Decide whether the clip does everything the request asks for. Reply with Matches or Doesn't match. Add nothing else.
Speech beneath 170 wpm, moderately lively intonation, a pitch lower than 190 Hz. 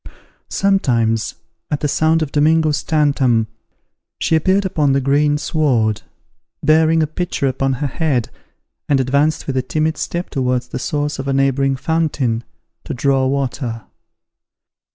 Matches